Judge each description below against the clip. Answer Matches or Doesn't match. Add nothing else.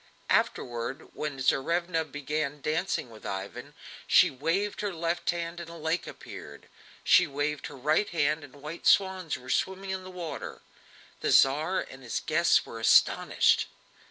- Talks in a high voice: Doesn't match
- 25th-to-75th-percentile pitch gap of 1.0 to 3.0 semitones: Doesn't match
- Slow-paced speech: Doesn't match